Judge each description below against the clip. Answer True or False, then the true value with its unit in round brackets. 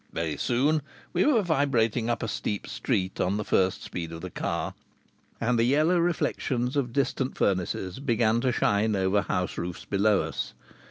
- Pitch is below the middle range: True (115 Hz)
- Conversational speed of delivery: True (170 wpm)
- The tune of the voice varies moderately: False (6.1 semitones)